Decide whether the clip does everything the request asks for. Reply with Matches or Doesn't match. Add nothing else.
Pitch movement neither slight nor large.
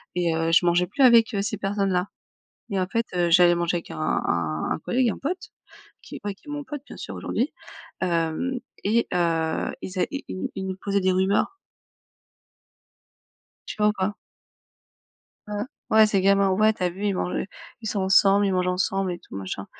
Matches